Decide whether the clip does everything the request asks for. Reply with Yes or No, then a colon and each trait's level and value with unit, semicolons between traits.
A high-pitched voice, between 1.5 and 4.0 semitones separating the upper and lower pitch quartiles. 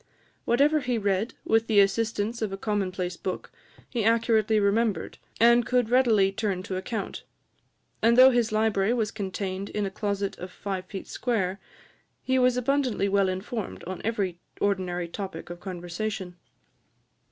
Yes: high, 205 Hz; average, 3.4 semitones